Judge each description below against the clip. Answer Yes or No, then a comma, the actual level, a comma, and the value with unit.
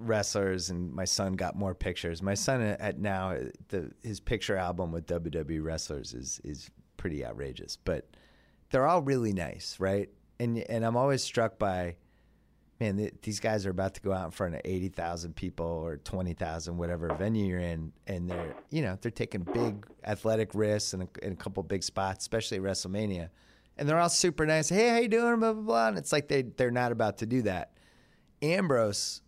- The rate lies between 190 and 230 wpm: Yes, average, 200 wpm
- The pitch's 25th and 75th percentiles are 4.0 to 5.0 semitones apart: Yes, average, 4.4 semitones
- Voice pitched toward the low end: Yes, low, 100 Hz